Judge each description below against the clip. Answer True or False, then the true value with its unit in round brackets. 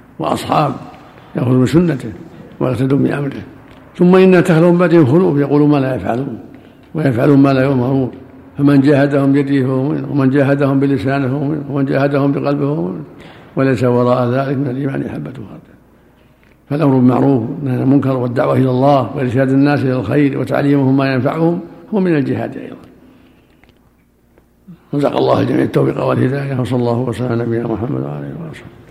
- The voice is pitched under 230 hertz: True (140 Hz)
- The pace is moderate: False (155 wpm)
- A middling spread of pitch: False (1.9 semitones)